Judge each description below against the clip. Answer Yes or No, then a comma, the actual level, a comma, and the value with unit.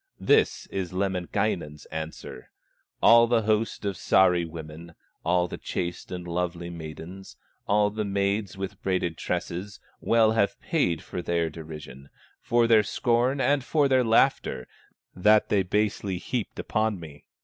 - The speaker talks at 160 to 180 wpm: No, average, 140 wpm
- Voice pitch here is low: Yes, very low, 95 Hz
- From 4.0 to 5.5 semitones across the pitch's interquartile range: Yes, average, 4.3 semitones